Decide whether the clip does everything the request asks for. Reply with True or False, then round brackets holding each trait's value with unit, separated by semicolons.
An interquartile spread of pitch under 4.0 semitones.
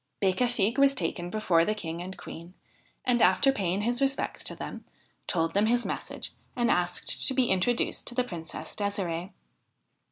False (5.4 semitones)